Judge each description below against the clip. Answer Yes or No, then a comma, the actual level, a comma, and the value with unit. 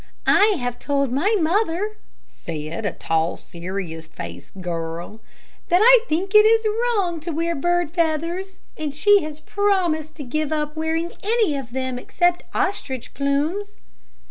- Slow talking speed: No, average, 145 wpm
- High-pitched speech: Yes, very high, 315 Hz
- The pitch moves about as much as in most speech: No, wide, 7.0 semitones